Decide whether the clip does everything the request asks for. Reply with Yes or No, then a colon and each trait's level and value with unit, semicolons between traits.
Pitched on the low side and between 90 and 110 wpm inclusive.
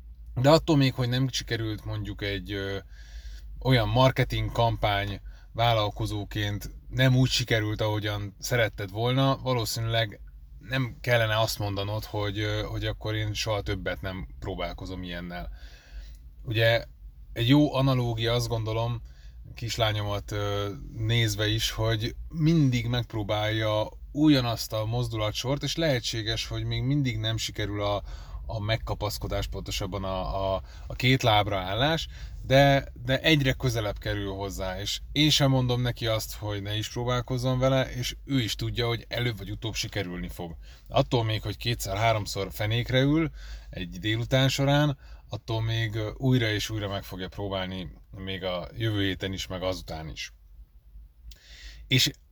No: low, 110 Hz; average, 135 wpm